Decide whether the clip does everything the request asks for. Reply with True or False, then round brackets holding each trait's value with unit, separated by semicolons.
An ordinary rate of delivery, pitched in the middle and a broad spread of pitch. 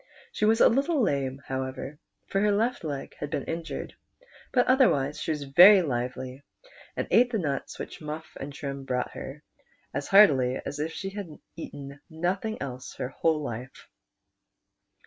True (165 wpm; 150 Hz; 6.4 semitones)